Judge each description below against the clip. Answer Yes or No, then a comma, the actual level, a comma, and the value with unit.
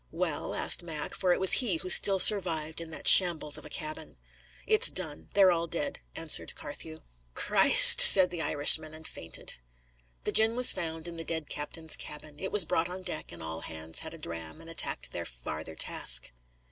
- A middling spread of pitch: Yes, average, 3.6 semitones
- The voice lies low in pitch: No, medium, 160 Hz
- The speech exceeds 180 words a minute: Yes, average, 195 wpm